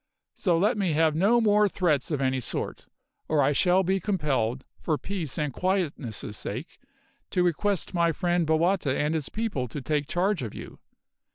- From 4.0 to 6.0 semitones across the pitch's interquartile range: Yes, average, 4.8 semitones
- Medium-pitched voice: Yes, medium, 165 Hz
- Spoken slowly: No, average, 175 wpm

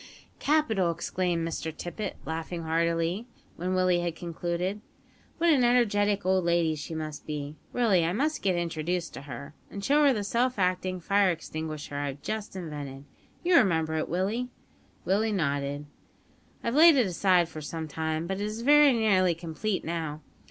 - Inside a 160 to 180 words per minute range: Yes, average, 165 wpm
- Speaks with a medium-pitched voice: Yes, medium, 175 Hz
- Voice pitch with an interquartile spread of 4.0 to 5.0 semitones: Yes, average, 4.6 semitones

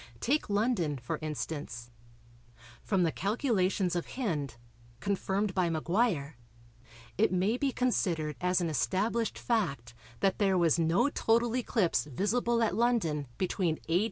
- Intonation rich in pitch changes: Yes, wide, 6.0 semitones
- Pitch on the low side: No, medium, 185 Hz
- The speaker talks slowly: Yes, slow, 130 wpm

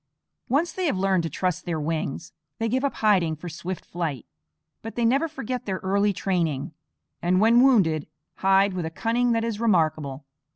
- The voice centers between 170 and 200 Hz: Yes, high, 190 Hz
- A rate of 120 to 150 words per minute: No, average, 180 wpm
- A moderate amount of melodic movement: No, wide, 5.8 semitones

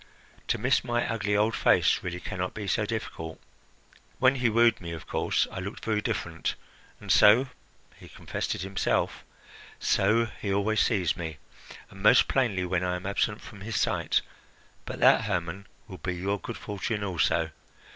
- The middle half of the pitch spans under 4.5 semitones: Yes, average, 3.5 semitones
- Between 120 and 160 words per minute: No, average, 175 wpm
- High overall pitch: No, low, 100 Hz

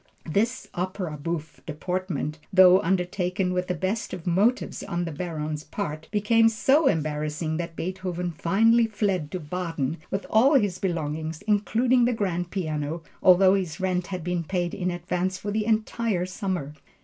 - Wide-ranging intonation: No, average, 3.4 semitones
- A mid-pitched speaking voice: Yes, medium, 180 Hz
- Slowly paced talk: No, average, 155 wpm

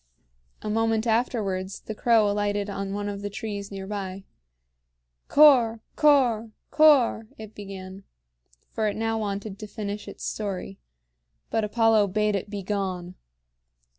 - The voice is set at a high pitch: Yes, high, 210 Hz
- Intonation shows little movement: Yes, narrow, 2.1 semitones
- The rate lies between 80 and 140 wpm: Yes, slow, 135 wpm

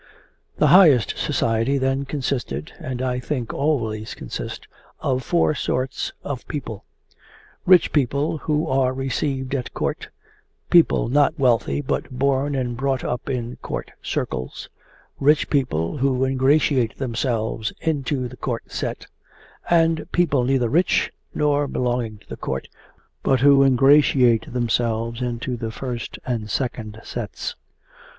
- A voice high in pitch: No, low, 130 Hz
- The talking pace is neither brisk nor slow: No, slow, 130 wpm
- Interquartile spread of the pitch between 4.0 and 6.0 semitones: No, average, 3.0 semitones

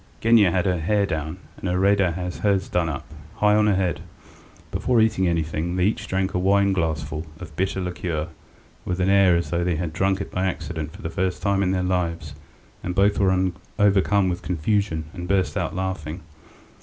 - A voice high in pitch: No, very low, 90 Hz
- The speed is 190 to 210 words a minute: Yes, average, 195 wpm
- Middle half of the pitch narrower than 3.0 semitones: Yes, narrow, 2.5 semitones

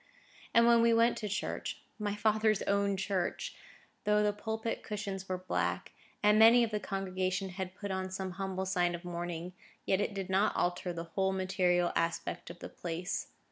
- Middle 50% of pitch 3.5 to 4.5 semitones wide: No, narrow, 2.4 semitones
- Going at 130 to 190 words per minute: Yes, average, 175 wpm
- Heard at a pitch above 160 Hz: Yes, high, 190 Hz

